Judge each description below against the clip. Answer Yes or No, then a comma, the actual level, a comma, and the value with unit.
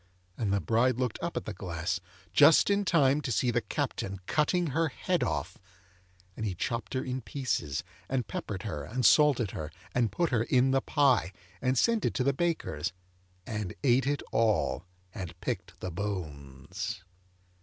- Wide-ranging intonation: Yes, wide, 6.6 semitones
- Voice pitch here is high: No, low, 120 Hz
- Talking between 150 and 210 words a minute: Yes, average, 175 wpm